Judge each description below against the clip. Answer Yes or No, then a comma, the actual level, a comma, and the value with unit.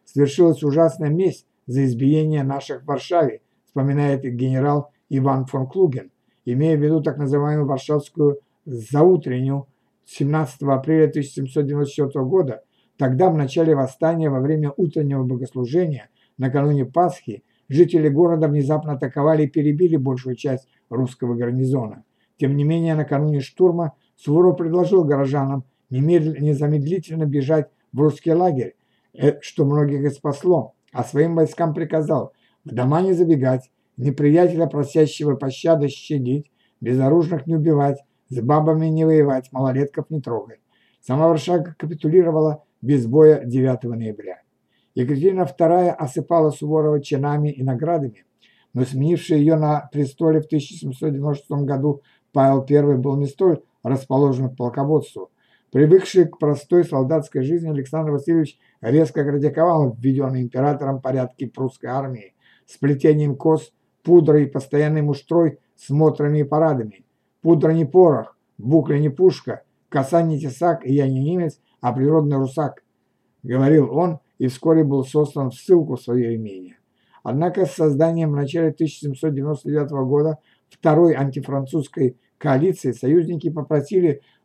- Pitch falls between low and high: Yes, medium, 145 Hz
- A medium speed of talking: Yes, average, 125 wpm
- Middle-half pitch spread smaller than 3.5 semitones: Yes, average, 2.9 semitones